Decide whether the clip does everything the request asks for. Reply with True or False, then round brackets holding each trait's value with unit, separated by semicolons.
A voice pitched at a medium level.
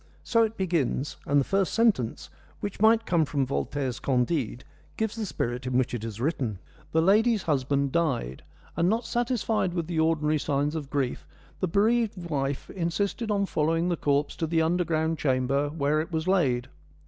True (160 Hz)